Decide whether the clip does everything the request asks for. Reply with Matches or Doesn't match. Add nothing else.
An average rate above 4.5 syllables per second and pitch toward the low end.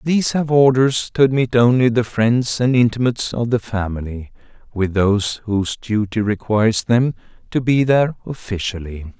Matches